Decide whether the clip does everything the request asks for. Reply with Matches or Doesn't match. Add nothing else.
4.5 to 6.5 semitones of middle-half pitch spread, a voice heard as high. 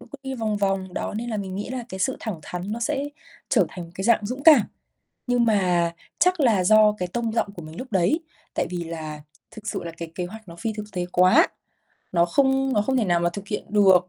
Matches